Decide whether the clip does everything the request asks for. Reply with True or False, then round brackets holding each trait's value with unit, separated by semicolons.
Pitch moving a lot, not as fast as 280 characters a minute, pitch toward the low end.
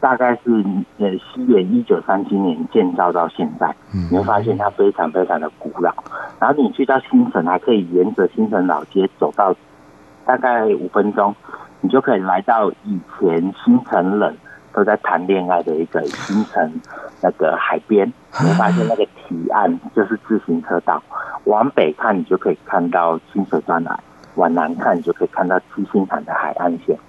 True (6.0 semitones; 265 characters per minute; 100 Hz)